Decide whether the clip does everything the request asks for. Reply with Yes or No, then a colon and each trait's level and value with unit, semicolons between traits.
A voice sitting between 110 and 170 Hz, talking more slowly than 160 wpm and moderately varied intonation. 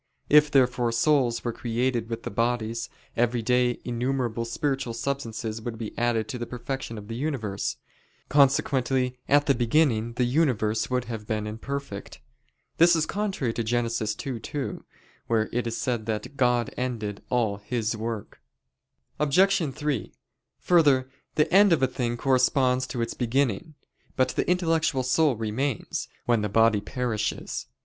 Yes: low, 120 Hz; average, 150 wpm; average, 3.2 semitones